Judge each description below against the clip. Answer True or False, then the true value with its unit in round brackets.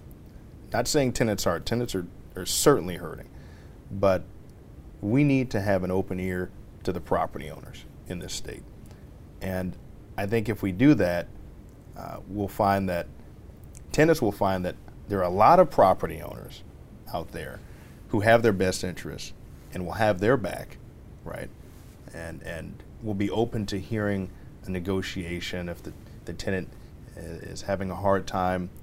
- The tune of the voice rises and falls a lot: False (3.2 semitones)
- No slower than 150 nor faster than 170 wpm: True (160 wpm)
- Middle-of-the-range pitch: False (95 Hz)